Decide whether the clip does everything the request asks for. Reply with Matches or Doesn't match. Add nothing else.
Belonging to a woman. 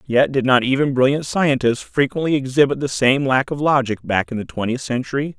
Doesn't match